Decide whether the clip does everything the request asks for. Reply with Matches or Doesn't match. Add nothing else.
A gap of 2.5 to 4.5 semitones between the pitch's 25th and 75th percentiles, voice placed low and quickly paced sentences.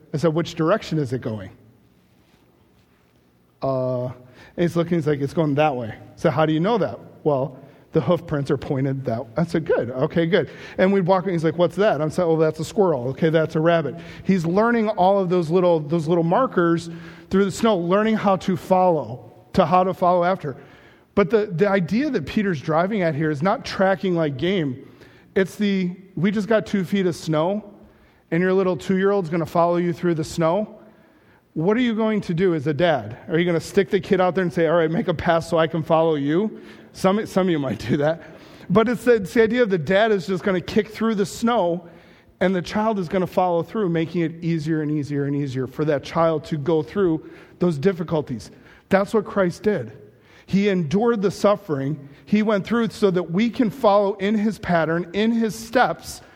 Doesn't match